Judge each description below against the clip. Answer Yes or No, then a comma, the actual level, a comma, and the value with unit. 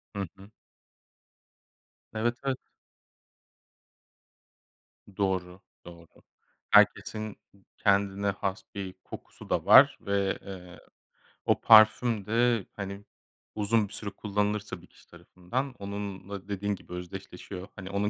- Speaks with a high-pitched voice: No, low, 100 Hz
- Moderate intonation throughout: No, narrow, 1.8 semitones